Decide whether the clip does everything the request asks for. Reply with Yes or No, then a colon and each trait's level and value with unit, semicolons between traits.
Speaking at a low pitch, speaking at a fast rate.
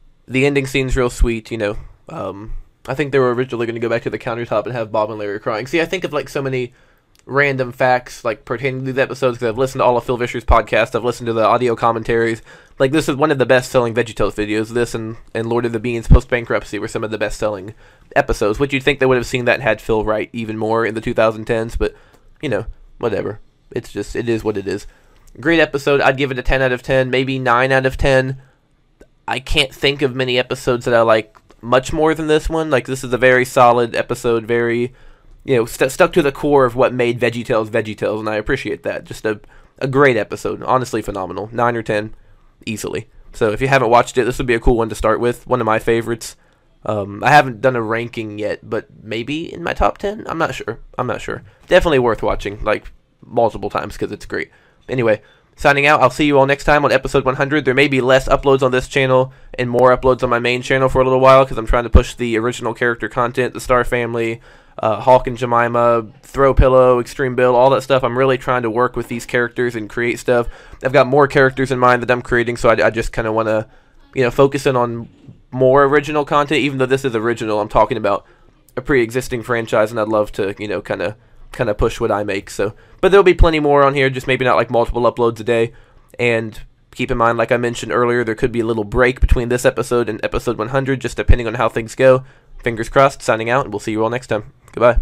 Yes: low, 125 Hz; fast, 245 wpm